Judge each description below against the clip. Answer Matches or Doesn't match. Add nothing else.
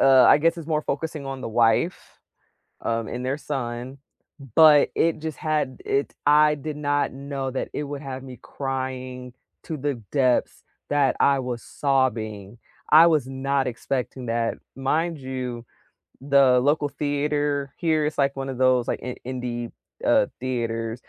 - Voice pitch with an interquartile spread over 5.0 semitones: Doesn't match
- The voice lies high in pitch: Doesn't match